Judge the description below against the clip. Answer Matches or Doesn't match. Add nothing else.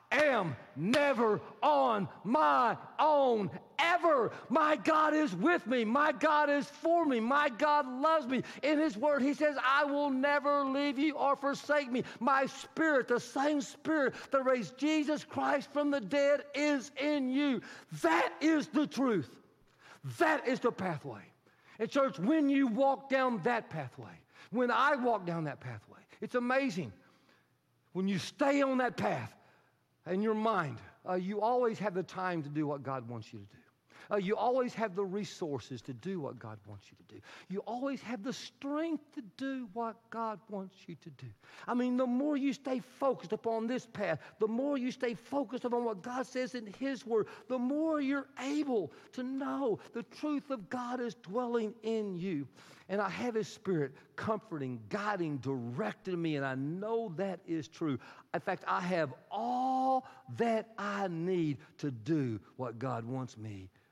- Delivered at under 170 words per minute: Doesn't match